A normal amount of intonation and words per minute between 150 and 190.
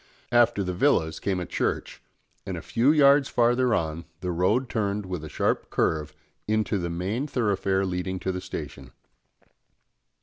Yes: average, 4.9 semitones; average, 160 wpm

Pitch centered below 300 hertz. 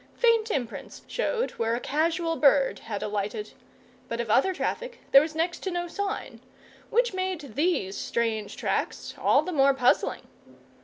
No: very high, 305 Hz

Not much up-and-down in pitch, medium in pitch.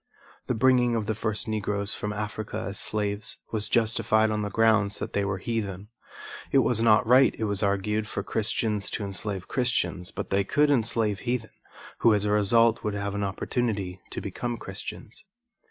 No: narrow, 2.1 semitones; low, 105 Hz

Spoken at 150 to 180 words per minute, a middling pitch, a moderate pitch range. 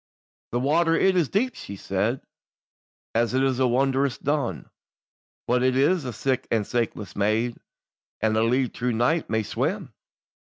No: average, 155 wpm; low, 125 Hz; average, 3.7 semitones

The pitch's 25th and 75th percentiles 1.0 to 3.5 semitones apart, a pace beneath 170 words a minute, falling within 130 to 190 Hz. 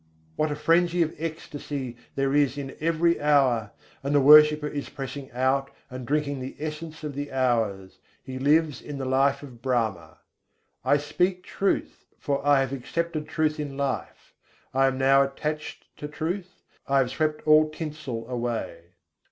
Yes: average, 2.7 semitones; average, 160 wpm; medium, 140 Hz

